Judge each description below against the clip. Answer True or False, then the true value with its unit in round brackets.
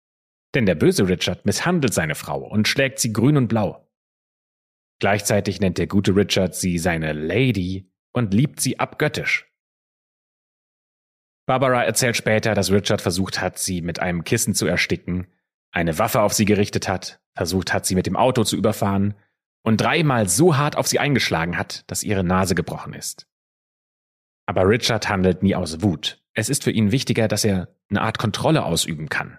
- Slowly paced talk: False (170 wpm)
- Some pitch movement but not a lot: True (3.5 semitones)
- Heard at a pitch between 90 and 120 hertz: True (100 Hz)